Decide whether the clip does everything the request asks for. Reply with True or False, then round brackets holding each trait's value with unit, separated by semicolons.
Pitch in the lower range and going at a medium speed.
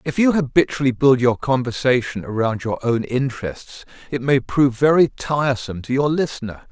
True (130 Hz; 160 wpm)